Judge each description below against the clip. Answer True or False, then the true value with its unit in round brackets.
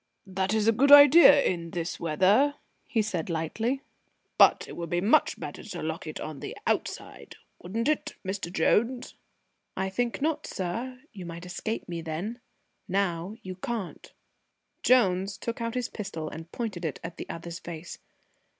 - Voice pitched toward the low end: False (190 Hz)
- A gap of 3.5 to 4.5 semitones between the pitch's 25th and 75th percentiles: False (5.6 semitones)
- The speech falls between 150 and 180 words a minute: True (165 wpm)